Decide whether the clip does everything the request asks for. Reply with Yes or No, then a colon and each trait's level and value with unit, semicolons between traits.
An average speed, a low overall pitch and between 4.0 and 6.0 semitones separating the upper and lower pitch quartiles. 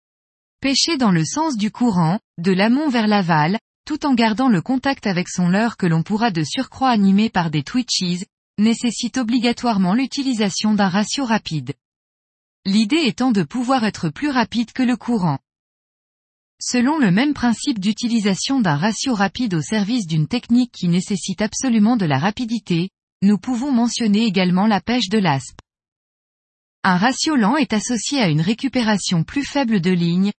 No: average, 160 wpm; high, 220 Hz; average, 5.1 semitones